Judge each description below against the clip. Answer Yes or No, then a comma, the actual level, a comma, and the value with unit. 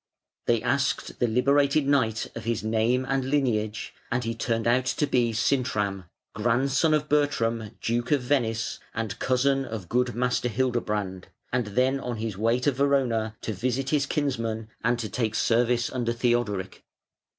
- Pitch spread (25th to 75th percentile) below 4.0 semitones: Yes, average, 2.9 semitones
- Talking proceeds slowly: No, average, 160 wpm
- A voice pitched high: No, low, 120 Hz